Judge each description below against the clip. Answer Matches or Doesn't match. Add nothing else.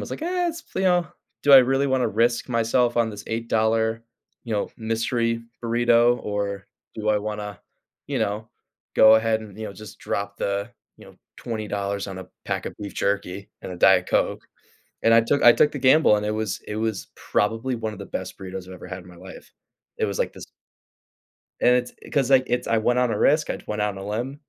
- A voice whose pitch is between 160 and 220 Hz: Doesn't match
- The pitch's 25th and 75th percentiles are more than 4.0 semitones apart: Doesn't match